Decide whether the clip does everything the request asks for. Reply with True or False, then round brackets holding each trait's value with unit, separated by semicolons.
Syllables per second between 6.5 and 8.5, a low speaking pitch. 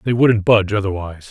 True (6.7 syllables/s; 105 Hz)